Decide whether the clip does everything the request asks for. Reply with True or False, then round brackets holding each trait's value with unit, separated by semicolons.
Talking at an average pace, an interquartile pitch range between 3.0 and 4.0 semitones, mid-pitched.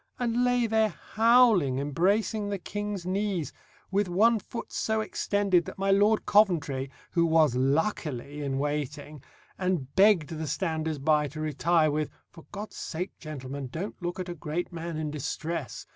False (160 wpm; 5.4 semitones; 170 Hz)